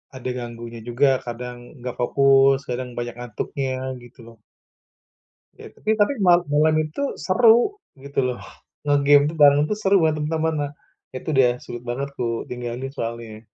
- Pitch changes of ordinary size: Yes, average, 3.3 semitones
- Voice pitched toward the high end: No, low, 135 Hz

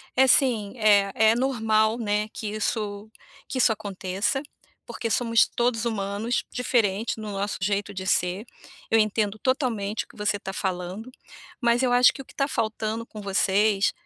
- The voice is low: No, high, 215 Hz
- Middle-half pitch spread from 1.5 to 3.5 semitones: Yes, narrow, 2.6 semitones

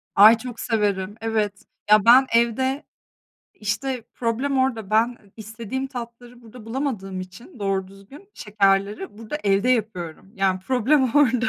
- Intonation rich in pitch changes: No, average, 4.0 semitones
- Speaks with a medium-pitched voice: No, high, 225 Hz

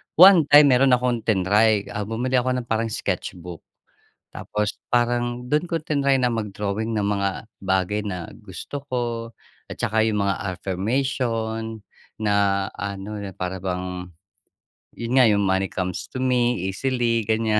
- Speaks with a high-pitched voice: No, low, 110 Hz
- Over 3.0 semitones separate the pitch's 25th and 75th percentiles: Yes, average, 3.9 semitones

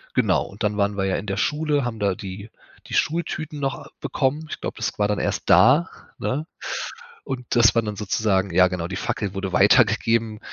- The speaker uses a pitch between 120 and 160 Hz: No, low, 110 Hz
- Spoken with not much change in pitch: No, average, 4.9 semitones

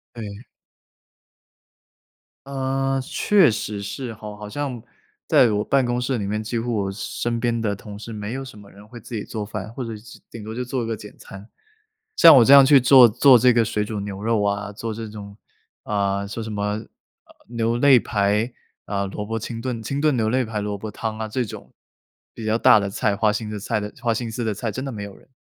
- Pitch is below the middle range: Yes, low, 110 Hz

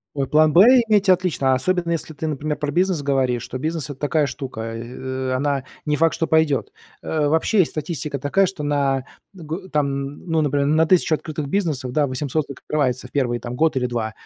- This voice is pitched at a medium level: Yes, medium, 145 Hz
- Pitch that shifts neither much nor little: Yes, average, 3.4 semitones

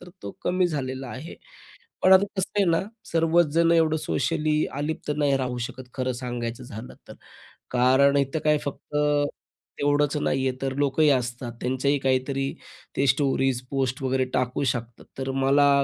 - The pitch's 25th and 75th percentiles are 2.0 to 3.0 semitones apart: Yes, average, 2.7 semitones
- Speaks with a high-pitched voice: No, low, 135 Hz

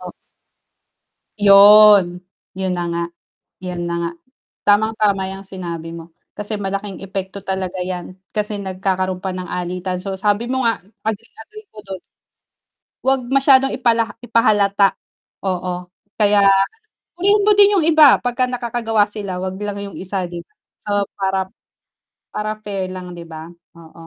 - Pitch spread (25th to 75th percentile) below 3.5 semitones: Yes, average, 2.9 semitones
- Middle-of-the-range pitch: No, high, 195 Hz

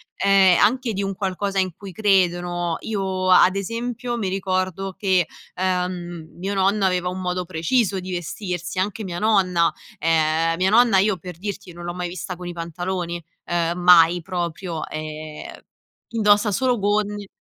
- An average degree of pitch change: No, narrow, 2.3 semitones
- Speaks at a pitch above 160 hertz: Yes, medium, 185 Hz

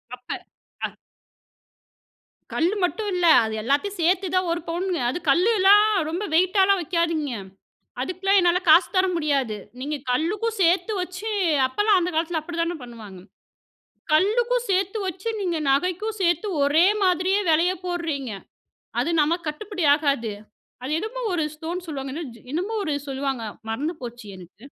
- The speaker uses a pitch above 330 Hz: Yes, very high, 340 Hz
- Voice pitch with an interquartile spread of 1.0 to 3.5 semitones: No, average, 4.5 semitones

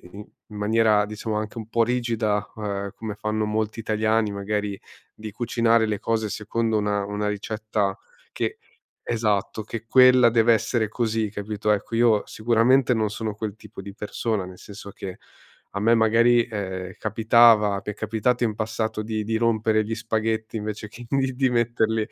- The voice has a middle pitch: No, low, 110 Hz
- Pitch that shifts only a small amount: Yes, narrow, 1.6 semitones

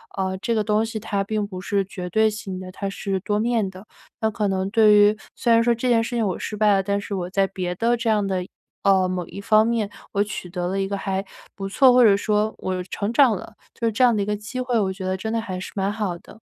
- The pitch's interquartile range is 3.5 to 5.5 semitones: No, narrow, 2.6 semitones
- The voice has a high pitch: Yes, high, 205 Hz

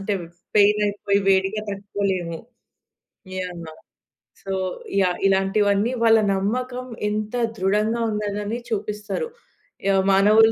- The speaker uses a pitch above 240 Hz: No, high, 205 Hz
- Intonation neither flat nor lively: No, narrow, 1.7 semitones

